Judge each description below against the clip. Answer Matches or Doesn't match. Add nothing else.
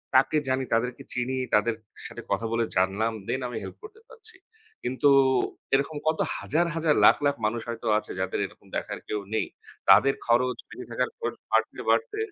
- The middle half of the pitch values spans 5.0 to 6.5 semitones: Matches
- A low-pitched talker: Matches